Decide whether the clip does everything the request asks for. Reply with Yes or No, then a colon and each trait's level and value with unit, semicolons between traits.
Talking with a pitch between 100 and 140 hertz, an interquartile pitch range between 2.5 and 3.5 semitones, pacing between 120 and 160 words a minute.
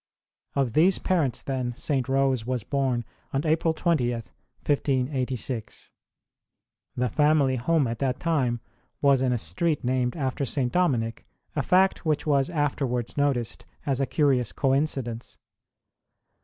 Yes: low, 135 Hz; average, 3.2 semitones; slow, 135 wpm